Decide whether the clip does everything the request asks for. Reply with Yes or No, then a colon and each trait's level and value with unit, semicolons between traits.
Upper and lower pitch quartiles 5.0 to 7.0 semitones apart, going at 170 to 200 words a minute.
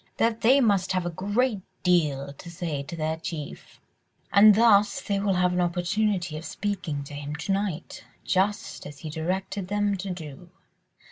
No: average, 4.2 semitones; average, 175 wpm